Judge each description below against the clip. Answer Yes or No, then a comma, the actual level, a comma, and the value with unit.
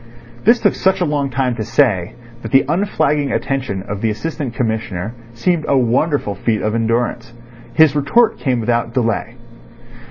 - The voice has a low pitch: Yes, low, 125 Hz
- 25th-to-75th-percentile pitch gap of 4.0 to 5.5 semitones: Yes, average, 4.5 semitones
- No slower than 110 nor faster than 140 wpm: No, average, 160 wpm